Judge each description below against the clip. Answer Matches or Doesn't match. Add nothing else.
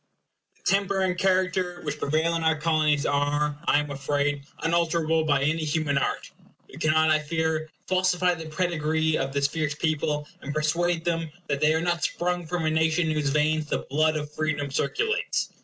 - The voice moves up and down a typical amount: Doesn't match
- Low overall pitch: Doesn't match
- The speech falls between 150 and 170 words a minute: Doesn't match